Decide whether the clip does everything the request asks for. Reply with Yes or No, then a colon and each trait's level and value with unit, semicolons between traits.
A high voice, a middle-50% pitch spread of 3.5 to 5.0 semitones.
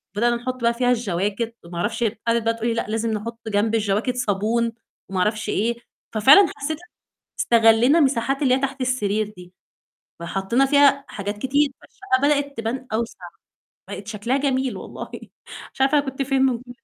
Yes: high, 235 Hz; average, 3.8 semitones